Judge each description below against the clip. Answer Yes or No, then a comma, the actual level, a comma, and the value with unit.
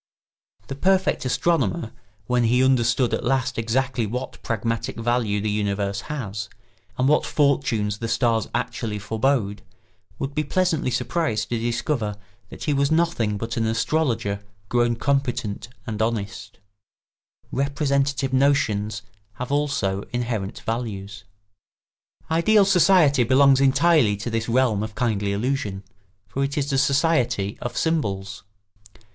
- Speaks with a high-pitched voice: No, low, 120 Hz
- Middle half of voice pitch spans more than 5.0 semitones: No, average, 4.6 semitones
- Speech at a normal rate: No, slow, 130 wpm